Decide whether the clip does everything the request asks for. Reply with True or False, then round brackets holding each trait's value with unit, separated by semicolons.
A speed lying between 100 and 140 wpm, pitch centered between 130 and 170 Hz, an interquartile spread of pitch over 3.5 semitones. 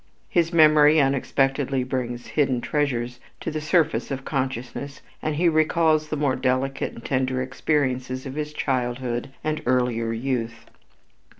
False (135 wpm; 135 Hz; 3.1 semitones)